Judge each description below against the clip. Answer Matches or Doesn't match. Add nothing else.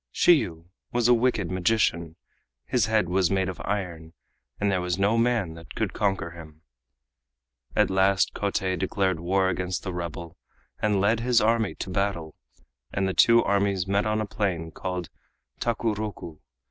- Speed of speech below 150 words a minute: Doesn't match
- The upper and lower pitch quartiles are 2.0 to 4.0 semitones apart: Matches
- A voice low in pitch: Matches